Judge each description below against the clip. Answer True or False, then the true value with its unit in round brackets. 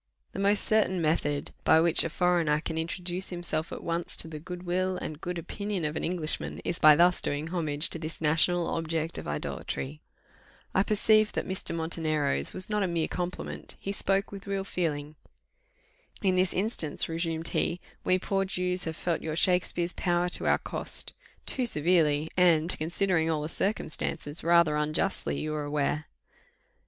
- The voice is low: False (170 Hz)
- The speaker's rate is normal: True (170 wpm)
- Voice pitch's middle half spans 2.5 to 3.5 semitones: True (2.8 semitones)